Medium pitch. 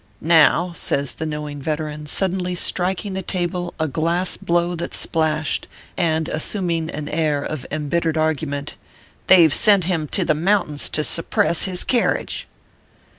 Yes: medium, 165 Hz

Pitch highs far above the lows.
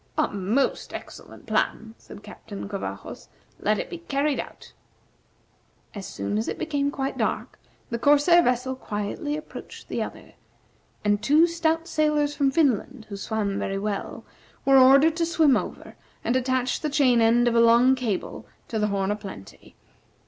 Yes: wide, 5.8 semitones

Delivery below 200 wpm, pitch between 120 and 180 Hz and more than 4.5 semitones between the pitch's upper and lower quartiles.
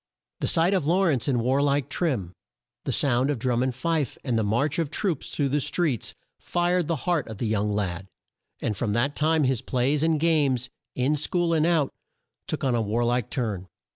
No: fast, 205 wpm; low, 135 Hz; average, 5.1 semitones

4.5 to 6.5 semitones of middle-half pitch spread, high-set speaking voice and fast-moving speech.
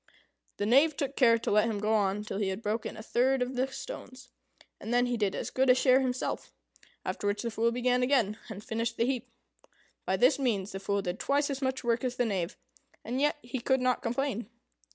No: average, 3.5 semitones; high, 240 Hz; fast, 225 wpm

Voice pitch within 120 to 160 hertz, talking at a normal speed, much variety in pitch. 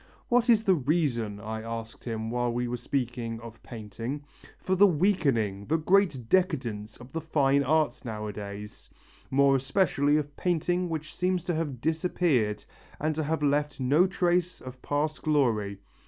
Yes: medium, 140 Hz; average, 155 wpm; wide, 6.0 semitones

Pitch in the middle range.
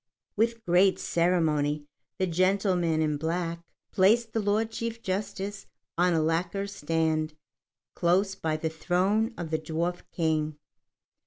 Yes: medium, 175 Hz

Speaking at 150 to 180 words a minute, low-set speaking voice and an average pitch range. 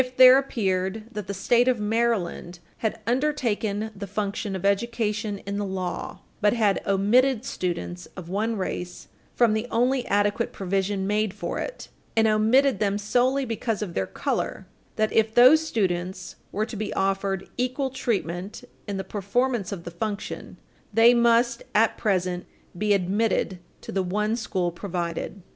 No: average, 160 wpm; high, 210 Hz; average, 3.4 semitones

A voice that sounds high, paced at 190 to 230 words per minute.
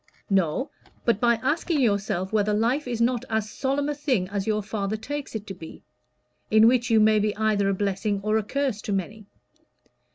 Yes: high, 215 Hz; average, 195 wpm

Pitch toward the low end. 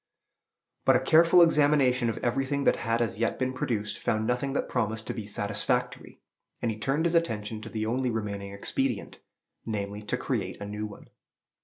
Yes: low, 115 Hz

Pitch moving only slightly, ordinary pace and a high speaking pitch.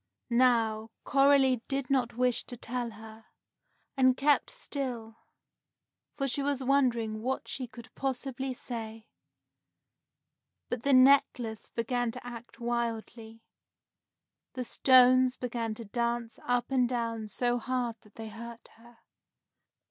No: narrow, 2.1 semitones; slow, 125 wpm; high, 245 Hz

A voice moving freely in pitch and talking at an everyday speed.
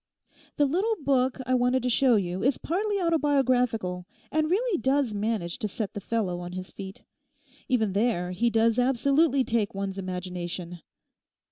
Yes: wide, 6.3 semitones; average, 155 wpm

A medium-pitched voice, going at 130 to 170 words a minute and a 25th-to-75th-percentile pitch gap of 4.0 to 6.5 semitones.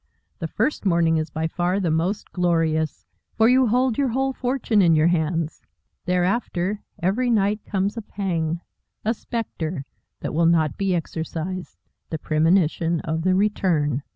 Yes: medium, 180 Hz; average, 155 wpm; average, 4.4 semitones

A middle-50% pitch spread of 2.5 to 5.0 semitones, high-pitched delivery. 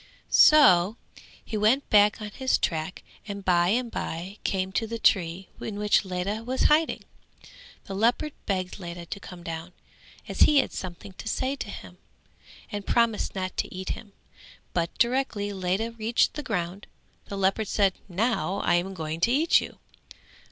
Yes: average, 4.0 semitones; high, 200 Hz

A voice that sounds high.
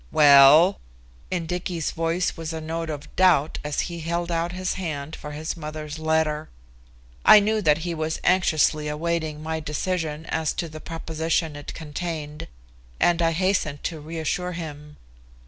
No: medium, 160 Hz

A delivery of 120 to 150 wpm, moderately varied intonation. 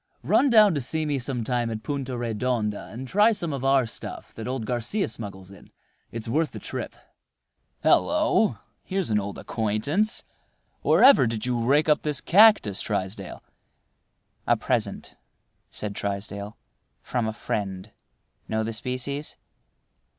No: average, 145 wpm; wide, 5.8 semitones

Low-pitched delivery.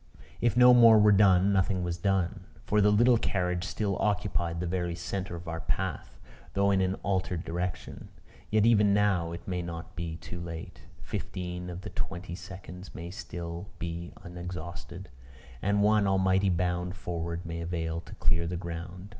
Yes: very low, 90 Hz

